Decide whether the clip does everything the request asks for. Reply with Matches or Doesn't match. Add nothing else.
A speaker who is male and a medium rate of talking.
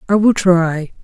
Doesn't match